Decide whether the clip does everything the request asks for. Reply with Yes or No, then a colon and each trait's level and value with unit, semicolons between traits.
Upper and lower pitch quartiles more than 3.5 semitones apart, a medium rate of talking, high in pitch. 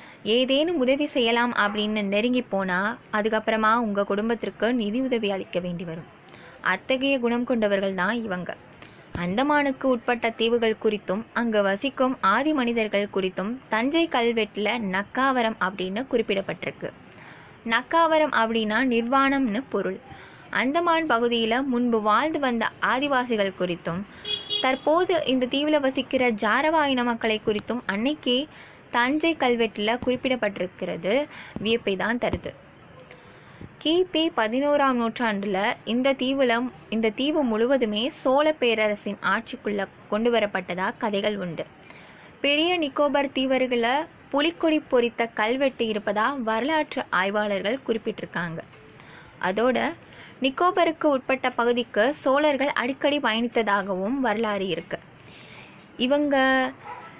Yes: average, 4.3 semitones; average, 95 wpm; high, 235 Hz